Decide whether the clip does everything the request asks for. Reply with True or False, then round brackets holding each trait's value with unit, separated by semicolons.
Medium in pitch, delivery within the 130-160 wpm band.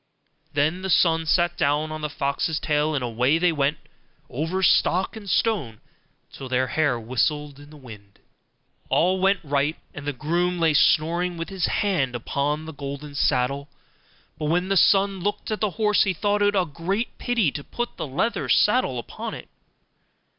False (155 Hz; 175 wpm)